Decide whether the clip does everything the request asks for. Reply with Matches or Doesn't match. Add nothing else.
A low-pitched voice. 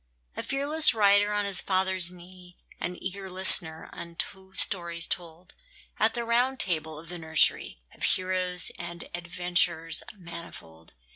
Doesn't match